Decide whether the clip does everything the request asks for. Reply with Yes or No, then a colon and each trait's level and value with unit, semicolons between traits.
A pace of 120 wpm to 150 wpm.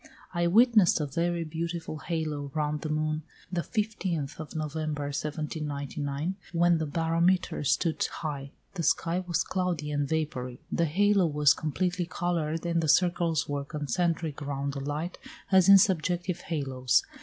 Yes: average, 145 wpm